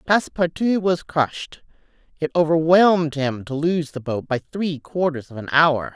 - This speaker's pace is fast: No, average, 160 wpm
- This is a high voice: No, medium, 155 Hz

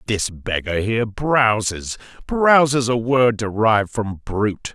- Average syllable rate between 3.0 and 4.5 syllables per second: Yes, 4.0 syllables/s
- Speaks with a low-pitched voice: Yes, low, 115 Hz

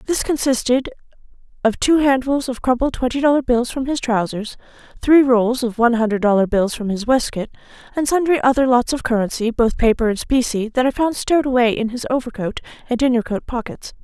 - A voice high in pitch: Yes, high, 245 Hz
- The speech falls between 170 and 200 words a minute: Yes, average, 190 wpm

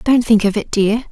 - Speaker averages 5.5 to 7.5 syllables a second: No, 4.8 syllables/s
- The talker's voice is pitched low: No, high, 220 Hz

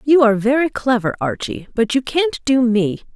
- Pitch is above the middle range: Yes, high, 245 Hz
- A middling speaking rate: Yes, average, 190 wpm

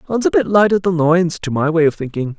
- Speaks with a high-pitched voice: No, medium, 165 Hz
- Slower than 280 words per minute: No, fast, 300 wpm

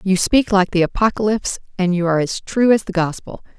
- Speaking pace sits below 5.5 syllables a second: No, 5.9 syllables/s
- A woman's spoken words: Yes, female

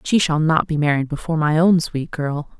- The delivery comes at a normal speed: No, fast, 255 wpm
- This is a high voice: No, medium, 155 Hz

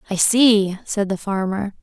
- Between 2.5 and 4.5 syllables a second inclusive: Yes, 4.0 syllables/s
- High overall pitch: Yes, high, 205 Hz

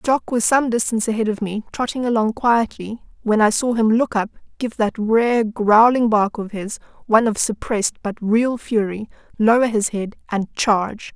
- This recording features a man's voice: No, female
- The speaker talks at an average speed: Yes, average, 170 wpm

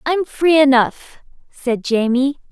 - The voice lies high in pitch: Yes, very high, 270 Hz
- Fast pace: No, slow, 120 wpm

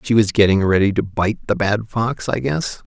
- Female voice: No, male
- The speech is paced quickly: Yes, fast, 225 wpm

